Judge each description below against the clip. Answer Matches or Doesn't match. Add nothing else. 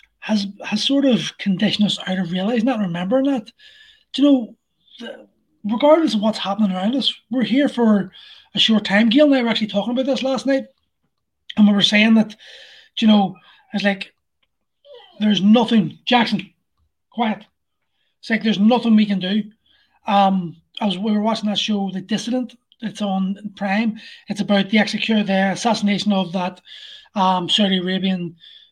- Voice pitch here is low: Doesn't match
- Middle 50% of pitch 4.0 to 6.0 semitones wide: Doesn't match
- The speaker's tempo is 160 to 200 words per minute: Matches